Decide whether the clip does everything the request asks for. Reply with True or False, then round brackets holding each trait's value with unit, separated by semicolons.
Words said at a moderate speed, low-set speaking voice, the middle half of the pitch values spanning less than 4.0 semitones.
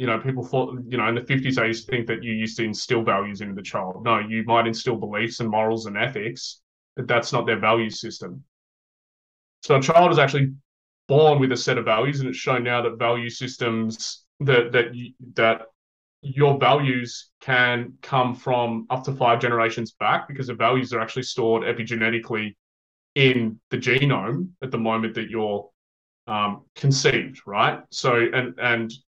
True (185 wpm; 115 Hz; 2.4 semitones)